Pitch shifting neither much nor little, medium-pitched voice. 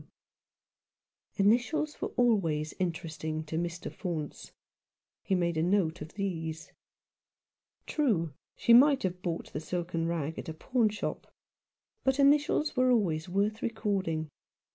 No: wide, 6.0 semitones; medium, 180 Hz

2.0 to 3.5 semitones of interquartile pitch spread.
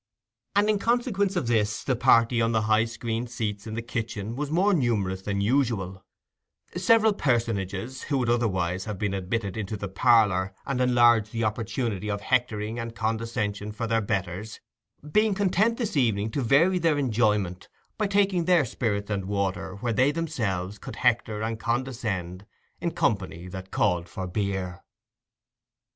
No: average, 4.4 semitones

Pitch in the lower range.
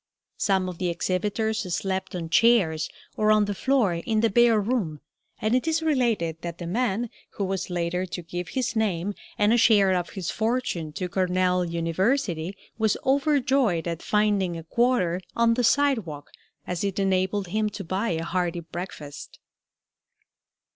No: high, 190 Hz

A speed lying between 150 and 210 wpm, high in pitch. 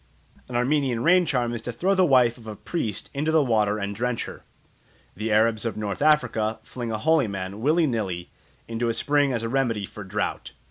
No: fast, 205 wpm; low, 115 Hz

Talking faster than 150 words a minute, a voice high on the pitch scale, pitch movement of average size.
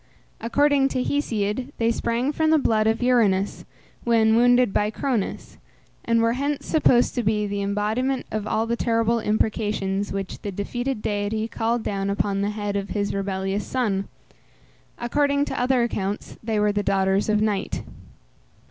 Yes: average, 160 wpm; high, 220 Hz; average, 3.2 semitones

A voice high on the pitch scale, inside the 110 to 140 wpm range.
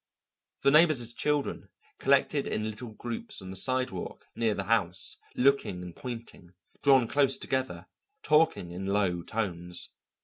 No: low, 115 Hz; slow, 135 wpm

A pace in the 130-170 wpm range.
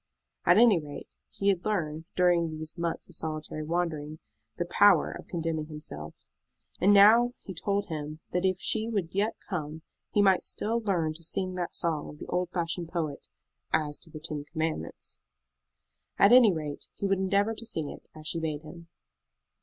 No: average, 180 wpm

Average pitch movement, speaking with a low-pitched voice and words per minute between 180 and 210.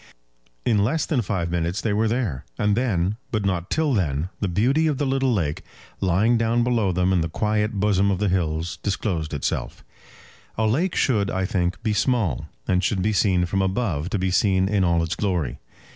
Yes: average, 4.0 semitones; low, 100 Hz; average, 200 wpm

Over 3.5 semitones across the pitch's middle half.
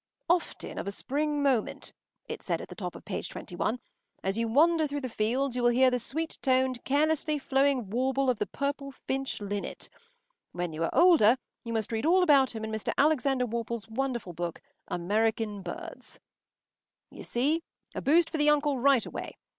Yes: average, 4.5 semitones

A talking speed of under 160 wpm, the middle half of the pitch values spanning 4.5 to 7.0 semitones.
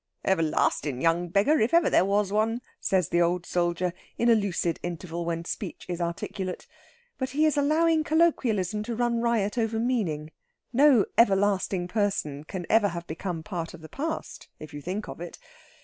No: average, 175 wpm; average, 5.3 semitones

